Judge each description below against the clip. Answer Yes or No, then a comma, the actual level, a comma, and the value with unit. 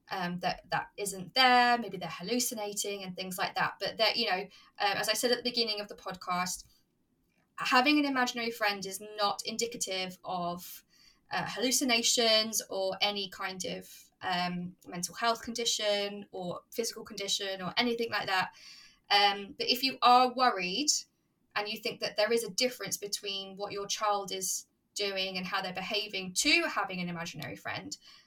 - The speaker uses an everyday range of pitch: Yes, average, 3.7 semitones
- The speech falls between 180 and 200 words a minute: No, average, 170 wpm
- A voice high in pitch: Yes, high, 205 Hz